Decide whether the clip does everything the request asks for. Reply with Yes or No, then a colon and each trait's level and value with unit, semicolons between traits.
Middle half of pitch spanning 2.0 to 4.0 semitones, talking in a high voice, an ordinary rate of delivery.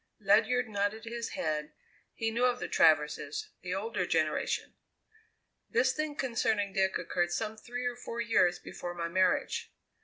No: average, 5.0 semitones; high, 210 Hz; average, 150 wpm